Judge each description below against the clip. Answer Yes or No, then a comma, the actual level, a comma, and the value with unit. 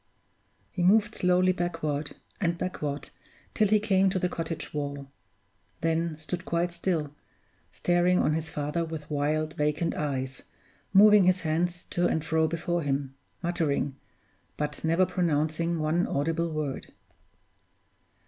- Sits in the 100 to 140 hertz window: No, medium, 165 Hz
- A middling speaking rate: No, slow, 130 wpm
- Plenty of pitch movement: No, average, 2.9 semitones